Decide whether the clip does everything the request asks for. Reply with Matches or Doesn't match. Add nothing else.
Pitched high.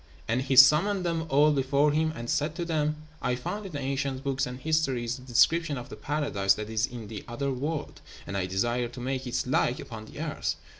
Doesn't match